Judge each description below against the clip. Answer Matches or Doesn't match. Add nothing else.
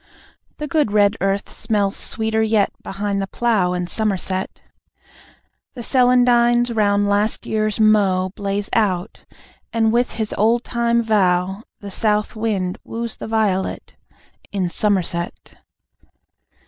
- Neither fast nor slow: Doesn't match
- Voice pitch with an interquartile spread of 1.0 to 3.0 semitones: Matches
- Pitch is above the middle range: Matches